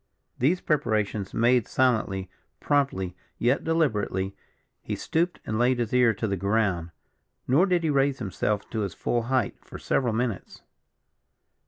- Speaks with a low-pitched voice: Yes, low, 120 Hz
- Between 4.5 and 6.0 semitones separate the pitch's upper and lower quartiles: Yes, average, 5.0 semitones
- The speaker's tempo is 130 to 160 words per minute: Yes, average, 145 wpm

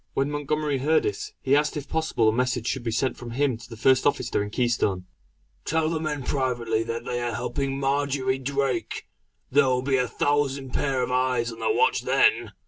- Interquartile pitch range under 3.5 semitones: Yes, average, 3.1 semitones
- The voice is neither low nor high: No, low, 130 Hz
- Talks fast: Yes, fast, 215 wpm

